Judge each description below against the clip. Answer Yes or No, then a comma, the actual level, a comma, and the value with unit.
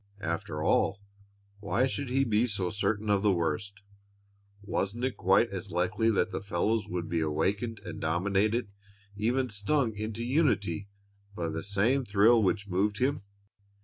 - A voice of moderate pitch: No, low, 105 Hz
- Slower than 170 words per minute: Yes, average, 150 wpm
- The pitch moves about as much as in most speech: Yes, average, 3.3 semitones